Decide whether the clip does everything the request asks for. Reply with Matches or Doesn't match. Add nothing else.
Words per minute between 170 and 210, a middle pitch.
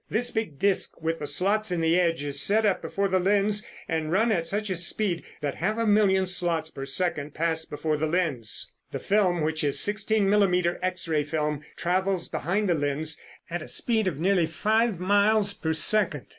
Matches